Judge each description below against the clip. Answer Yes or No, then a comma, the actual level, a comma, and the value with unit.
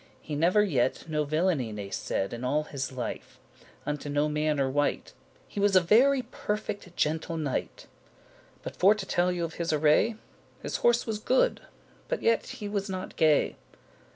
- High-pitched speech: No, medium, 160 Hz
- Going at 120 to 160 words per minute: No, average, 170 wpm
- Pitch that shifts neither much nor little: No, wide, 5.8 semitones